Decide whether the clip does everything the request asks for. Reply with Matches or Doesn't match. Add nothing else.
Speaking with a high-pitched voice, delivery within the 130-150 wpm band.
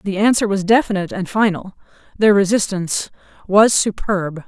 Matches